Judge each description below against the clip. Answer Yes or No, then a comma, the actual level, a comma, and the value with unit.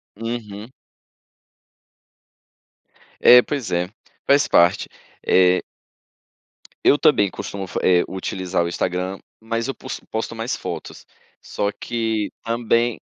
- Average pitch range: Yes, average, 4.0 semitones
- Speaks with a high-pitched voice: No, low, 110 Hz